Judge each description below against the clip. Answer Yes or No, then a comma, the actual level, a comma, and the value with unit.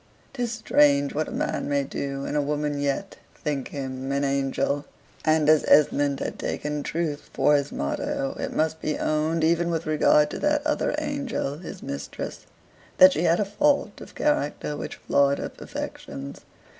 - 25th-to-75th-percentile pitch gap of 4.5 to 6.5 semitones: No, average, 3.0 semitones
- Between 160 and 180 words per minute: Yes, average, 170 wpm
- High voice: No, medium, 150 Hz